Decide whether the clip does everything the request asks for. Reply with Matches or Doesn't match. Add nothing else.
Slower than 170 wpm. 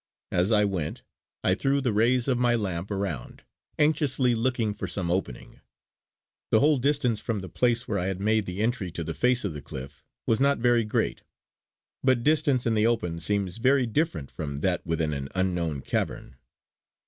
Doesn't match